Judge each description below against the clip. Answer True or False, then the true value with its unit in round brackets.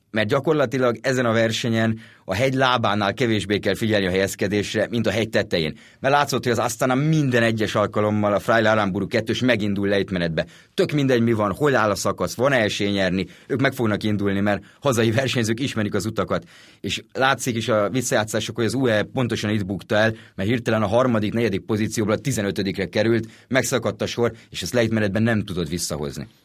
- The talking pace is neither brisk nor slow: False (190 wpm)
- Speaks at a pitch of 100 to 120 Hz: True (110 Hz)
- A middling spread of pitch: True (3.0 semitones)